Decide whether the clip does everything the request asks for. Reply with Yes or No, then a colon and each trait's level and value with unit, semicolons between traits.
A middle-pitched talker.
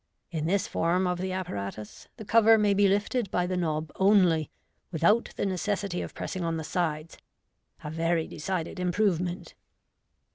Yes: medium, 180 Hz